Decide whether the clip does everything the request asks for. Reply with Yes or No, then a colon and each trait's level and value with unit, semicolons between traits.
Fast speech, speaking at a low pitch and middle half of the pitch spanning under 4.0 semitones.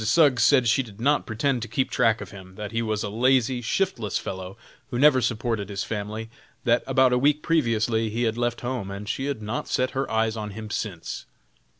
Yes: fast, 215 wpm; low, 115 Hz; average, 3.2 semitones